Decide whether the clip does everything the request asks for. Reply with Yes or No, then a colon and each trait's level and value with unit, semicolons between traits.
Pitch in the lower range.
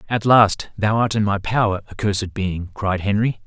Yes: low, 105 Hz